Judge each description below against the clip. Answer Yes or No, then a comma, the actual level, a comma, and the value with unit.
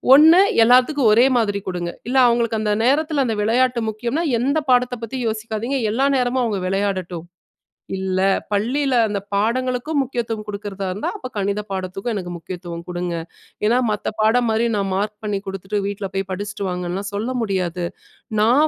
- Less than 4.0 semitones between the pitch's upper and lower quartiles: No, average, 4.3 semitones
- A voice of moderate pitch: No, high, 215 Hz